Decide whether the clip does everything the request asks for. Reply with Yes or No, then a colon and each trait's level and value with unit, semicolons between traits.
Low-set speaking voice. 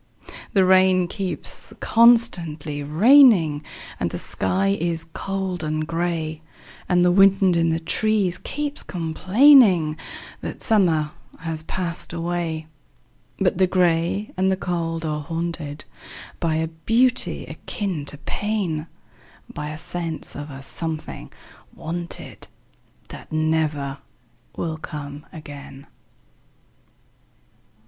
No: medium, 170 Hz